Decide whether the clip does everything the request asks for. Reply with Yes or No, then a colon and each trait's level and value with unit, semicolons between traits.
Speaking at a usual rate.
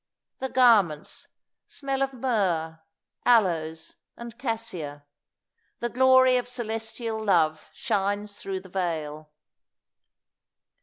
No: slow, 95 wpm